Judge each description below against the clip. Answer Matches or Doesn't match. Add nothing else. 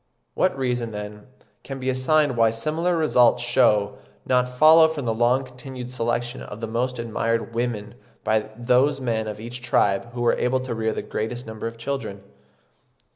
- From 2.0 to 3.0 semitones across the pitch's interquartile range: Matches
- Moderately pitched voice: Doesn't match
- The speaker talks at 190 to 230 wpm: Doesn't match